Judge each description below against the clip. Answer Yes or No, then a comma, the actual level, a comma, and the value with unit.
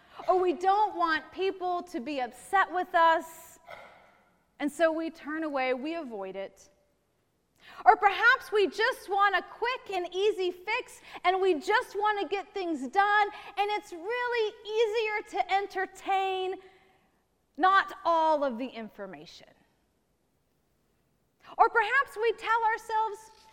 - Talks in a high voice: Yes, very high, 375 Hz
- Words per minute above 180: No, slow, 135 wpm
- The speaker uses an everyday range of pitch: Yes, average, 4.3 semitones